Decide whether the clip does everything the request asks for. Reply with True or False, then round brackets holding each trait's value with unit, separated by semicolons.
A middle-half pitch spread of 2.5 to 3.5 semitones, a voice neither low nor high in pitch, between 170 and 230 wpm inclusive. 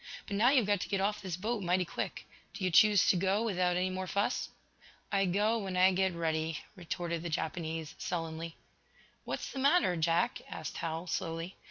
True (3.2 semitones; 180 Hz; 190 wpm)